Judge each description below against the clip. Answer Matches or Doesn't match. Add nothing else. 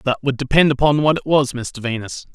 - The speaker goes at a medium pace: Doesn't match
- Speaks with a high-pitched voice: Doesn't match